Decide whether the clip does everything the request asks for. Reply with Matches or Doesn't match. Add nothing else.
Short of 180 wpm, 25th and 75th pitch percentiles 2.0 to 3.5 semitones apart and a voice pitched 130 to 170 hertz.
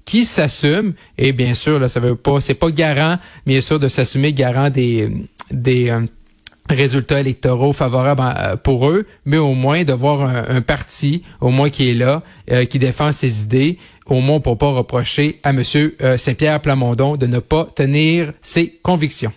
Doesn't match